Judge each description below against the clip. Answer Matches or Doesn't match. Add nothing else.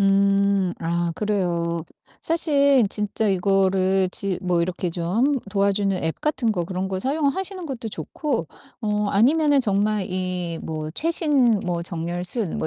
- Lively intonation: Doesn't match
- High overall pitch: Matches